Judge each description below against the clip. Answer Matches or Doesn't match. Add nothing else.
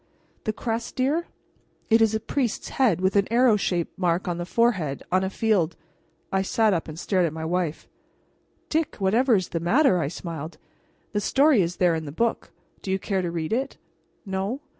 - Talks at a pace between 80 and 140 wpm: Doesn't match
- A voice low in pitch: Doesn't match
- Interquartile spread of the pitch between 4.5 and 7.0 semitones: Matches